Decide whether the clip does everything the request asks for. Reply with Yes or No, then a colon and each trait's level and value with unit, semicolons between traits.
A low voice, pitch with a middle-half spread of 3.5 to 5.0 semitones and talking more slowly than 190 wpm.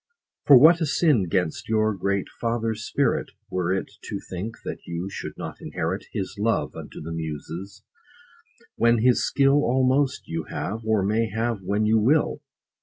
Yes: low, 110 Hz; average, 4.4 semitones; average, 165 wpm